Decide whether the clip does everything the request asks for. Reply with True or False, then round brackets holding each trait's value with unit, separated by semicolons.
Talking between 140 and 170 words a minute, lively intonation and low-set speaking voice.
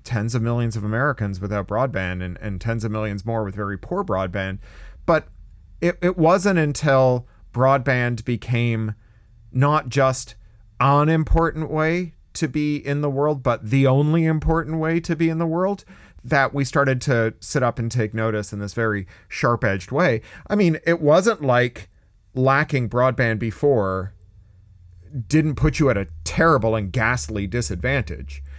True (160 wpm; 5.9 semitones; 120 Hz)